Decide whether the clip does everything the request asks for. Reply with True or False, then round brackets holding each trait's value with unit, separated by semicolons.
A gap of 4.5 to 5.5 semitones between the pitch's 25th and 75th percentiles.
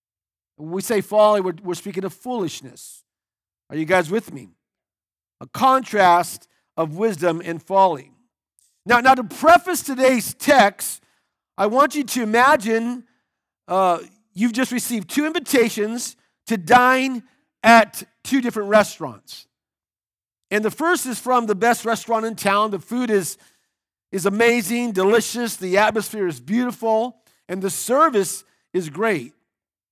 True (5.0 semitones)